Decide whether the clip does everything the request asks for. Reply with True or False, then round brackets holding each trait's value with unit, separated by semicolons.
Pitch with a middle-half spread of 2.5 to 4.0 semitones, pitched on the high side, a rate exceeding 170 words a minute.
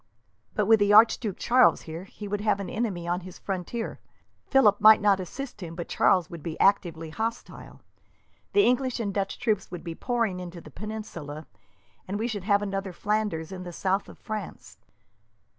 True (3.5 semitones; 200 Hz; 180 wpm)